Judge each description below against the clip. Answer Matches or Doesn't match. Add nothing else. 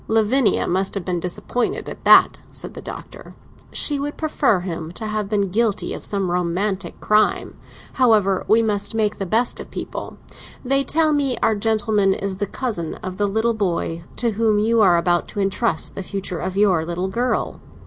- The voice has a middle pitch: Doesn't match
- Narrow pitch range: Doesn't match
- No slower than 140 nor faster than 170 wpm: Doesn't match